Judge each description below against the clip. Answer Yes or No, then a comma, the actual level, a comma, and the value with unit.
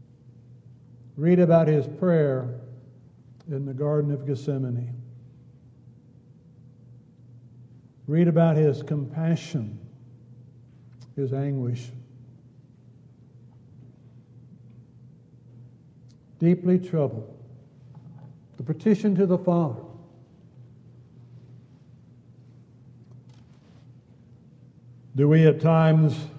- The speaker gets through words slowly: Yes, slow, 60 wpm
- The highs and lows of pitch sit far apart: No, average, 2.9 semitones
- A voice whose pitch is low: Yes, low, 130 Hz